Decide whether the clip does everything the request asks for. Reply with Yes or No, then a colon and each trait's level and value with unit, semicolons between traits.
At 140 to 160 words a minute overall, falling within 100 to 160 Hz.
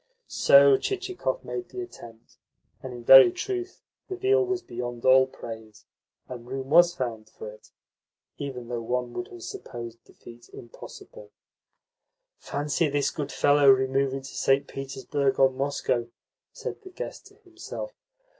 Yes: average, 145 wpm; low, 135 Hz